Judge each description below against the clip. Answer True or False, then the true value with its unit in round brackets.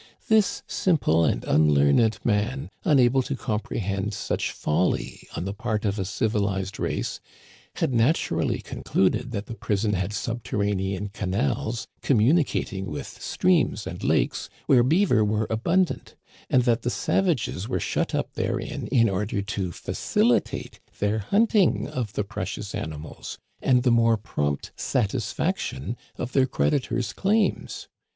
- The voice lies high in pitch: False (110 Hz)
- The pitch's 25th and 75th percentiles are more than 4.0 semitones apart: True (4.5 semitones)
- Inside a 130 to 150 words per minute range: True (140 wpm)